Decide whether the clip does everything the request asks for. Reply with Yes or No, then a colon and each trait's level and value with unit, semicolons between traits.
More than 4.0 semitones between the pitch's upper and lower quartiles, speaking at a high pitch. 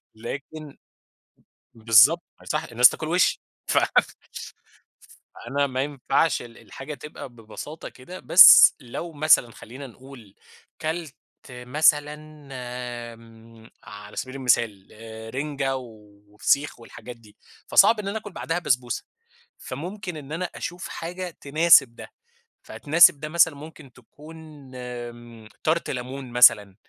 No: average, 4.7 semitones; low, 135 Hz